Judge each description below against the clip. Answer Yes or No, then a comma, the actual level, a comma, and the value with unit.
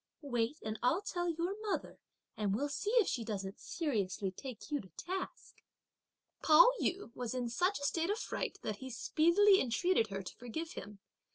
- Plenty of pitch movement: Yes, wide, 7.9 semitones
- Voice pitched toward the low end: No, very high, 270 Hz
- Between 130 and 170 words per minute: No, average, 180 wpm